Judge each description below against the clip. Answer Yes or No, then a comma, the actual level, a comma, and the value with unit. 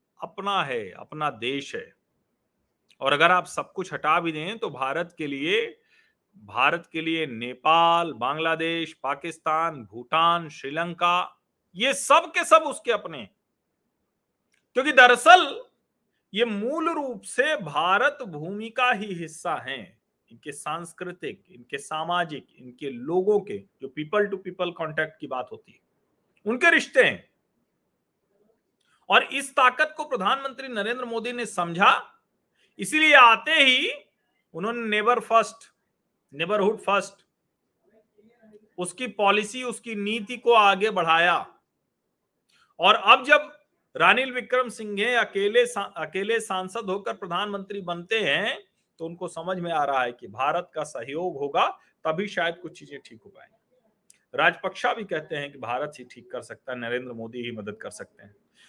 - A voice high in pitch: Yes, high, 200 Hz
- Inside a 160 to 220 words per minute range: No, average, 145 wpm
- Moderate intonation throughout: No, wide, 6.8 semitones